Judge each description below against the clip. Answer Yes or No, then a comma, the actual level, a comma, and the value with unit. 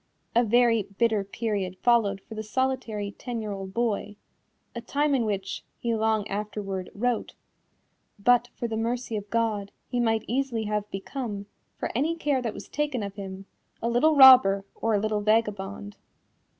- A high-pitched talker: Yes, high, 220 Hz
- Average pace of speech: Yes, average, 165 wpm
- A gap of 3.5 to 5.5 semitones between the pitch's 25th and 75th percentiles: No, average, 3.0 semitones